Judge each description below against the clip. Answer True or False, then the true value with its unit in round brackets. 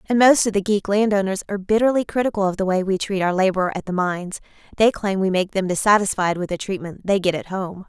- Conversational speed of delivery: False (245 wpm)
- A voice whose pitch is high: True (195 Hz)